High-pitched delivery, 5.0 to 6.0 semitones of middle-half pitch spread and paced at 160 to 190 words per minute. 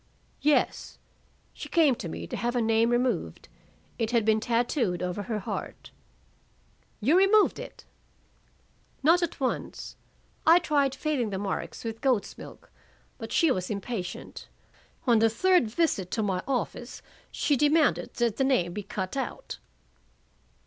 No: high, 240 Hz; average, 5.3 semitones; average, 145 wpm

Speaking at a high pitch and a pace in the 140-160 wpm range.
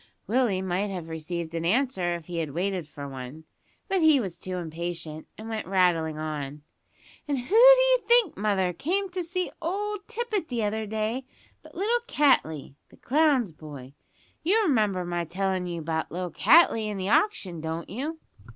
No: high, 195 Hz; average, 170 wpm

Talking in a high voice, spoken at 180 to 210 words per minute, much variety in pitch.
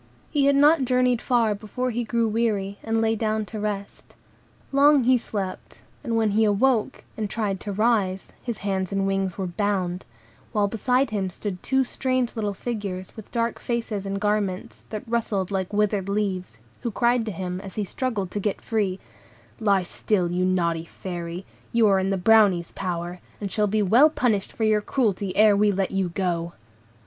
No: high, 205 Hz; average, 185 wpm; average, 3.2 semitones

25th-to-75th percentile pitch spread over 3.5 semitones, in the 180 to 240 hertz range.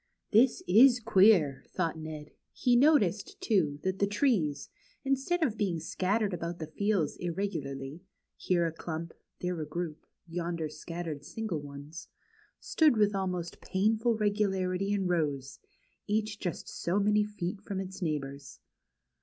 Yes: average, 4.8 semitones; medium, 185 Hz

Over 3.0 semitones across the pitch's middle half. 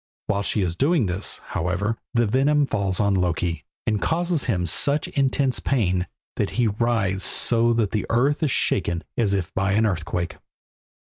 Yes: wide, 5.6 semitones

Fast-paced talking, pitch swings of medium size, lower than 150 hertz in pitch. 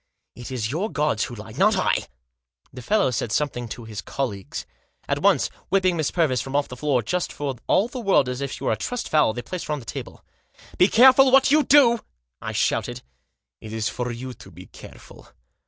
No: fast, 230 wpm; wide, 8.1 semitones; medium, 140 Hz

